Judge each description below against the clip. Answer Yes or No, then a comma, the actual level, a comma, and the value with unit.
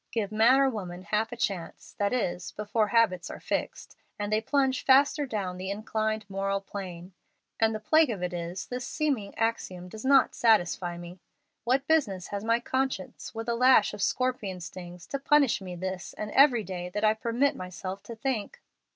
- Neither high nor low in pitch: No, high, 215 Hz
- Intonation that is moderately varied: Yes, average, 4.9 semitones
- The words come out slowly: No, average, 185 wpm